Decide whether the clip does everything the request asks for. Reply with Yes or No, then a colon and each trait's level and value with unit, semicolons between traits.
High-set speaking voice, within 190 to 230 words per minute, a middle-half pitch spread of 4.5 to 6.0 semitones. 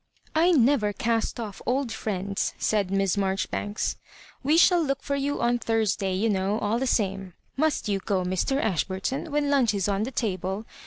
Yes: high, 215 Hz; fast, 205 wpm; wide, 5.5 semitones